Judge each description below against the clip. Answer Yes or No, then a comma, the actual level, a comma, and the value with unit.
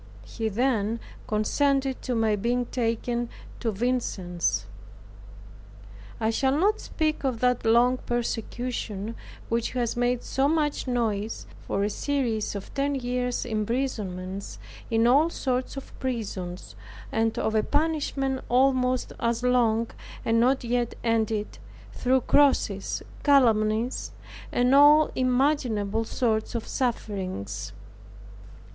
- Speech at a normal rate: No, slow, 115 wpm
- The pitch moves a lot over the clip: No, average, 3.1 semitones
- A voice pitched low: No, high, 240 Hz